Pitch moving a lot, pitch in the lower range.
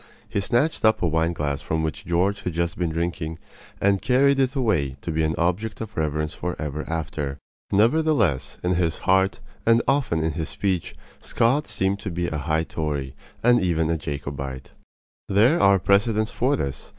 Yes: wide, 5.7 semitones; very low, 85 Hz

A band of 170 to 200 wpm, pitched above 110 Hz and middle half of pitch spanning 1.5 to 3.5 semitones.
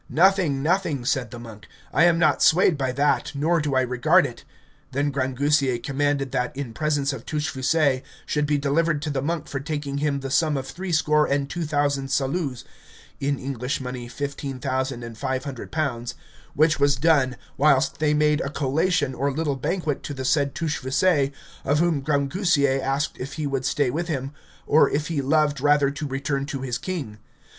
Yes: average, 185 wpm; medium, 140 Hz; narrow, 2.4 semitones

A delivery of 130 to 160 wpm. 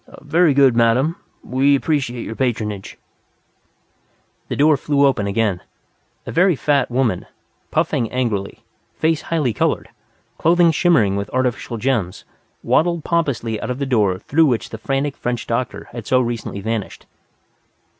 Yes: average, 140 wpm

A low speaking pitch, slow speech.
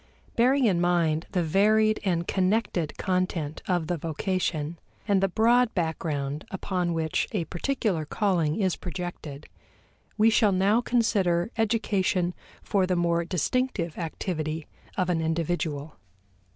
No: medium, 180 Hz; slow, 125 wpm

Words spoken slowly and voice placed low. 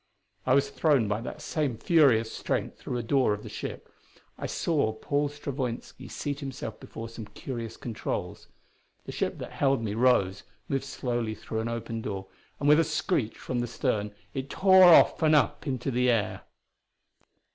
No: average, 175 wpm; low, 125 Hz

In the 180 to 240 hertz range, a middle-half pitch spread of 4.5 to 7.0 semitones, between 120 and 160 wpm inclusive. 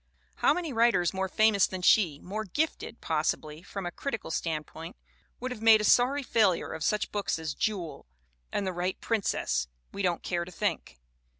No: high, 190 Hz; average, 4.8 semitones; average, 180 wpm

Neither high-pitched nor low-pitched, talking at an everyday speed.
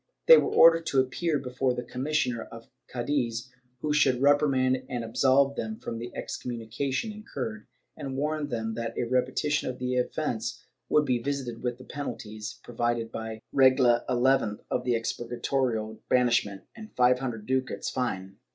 No: low, 125 Hz; average, 160 wpm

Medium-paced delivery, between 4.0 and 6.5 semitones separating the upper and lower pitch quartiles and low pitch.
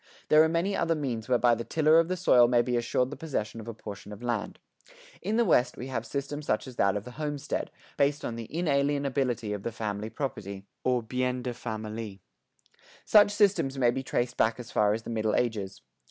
No: fast, 210 wpm; average, 4.7 semitones; low, 125 Hz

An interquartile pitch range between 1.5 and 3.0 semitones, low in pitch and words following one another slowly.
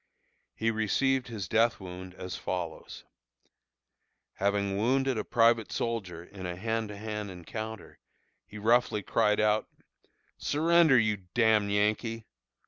Yes: narrow, 2.6 semitones; low, 110 Hz; slow, 130 wpm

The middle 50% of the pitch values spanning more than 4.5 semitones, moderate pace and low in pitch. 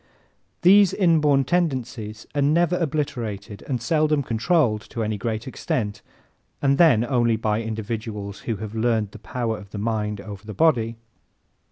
Yes: average, 5.2 semitones; average, 150 wpm; low, 115 Hz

